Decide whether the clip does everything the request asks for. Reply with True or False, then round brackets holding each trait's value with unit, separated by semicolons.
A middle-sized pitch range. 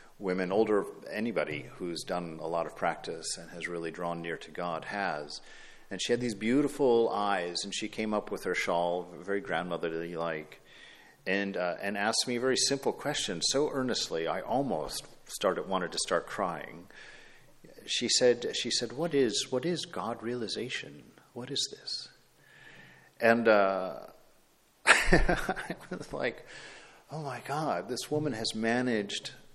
False (5.7 semitones)